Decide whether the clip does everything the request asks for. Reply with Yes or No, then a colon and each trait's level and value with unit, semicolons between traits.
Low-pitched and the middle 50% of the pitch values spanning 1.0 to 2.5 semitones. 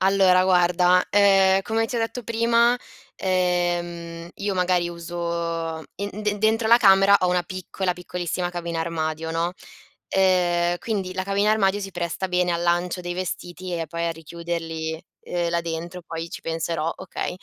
No: medium, 180 Hz; narrow, 2.2 semitones